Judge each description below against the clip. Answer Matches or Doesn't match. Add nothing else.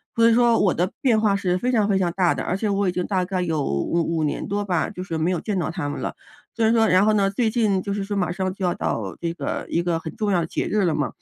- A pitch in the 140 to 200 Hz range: Matches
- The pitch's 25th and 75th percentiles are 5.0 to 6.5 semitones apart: Doesn't match